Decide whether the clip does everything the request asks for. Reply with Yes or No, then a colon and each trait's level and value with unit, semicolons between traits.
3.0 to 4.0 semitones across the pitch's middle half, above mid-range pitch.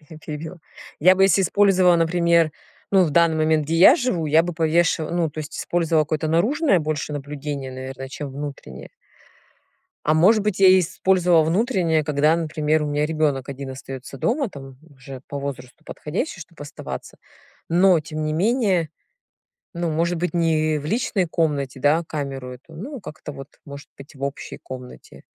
No: average, 3.4 semitones; medium, 155 Hz